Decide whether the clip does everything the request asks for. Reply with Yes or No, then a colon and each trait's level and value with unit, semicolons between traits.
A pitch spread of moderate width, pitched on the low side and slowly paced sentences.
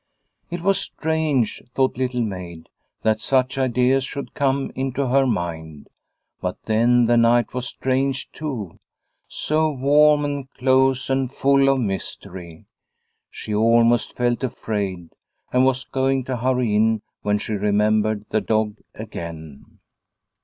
Yes: average, 4.0 semitones; low, 125 Hz; slow, 130 wpm